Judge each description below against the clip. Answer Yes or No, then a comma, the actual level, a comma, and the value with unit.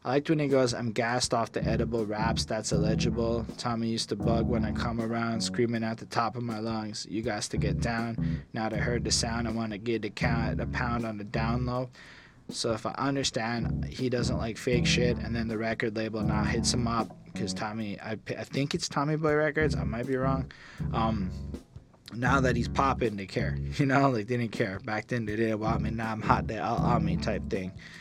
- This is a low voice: Yes, low, 115 Hz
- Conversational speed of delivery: No, fast, 235 wpm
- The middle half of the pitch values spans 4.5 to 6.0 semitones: No, narrow, 2.6 semitones